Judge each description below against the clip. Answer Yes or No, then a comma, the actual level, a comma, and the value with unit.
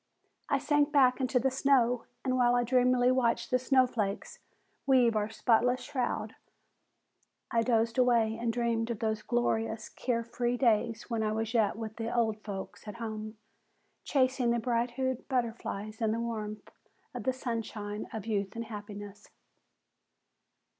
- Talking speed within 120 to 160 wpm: Yes, average, 150 wpm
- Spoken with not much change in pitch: Yes, narrow, 2.3 semitones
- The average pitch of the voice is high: Yes, high, 235 Hz